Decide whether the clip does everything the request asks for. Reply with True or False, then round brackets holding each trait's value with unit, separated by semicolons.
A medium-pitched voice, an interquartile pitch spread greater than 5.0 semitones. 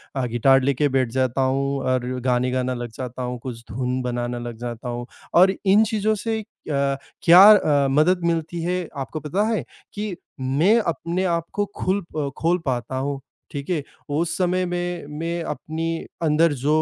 True (145 Hz; 5.4 semitones)